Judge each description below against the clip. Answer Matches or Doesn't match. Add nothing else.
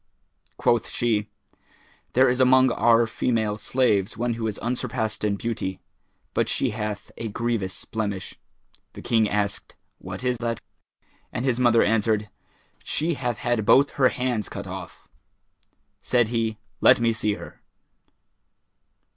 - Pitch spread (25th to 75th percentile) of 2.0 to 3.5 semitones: Matches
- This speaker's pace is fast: Doesn't match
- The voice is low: Matches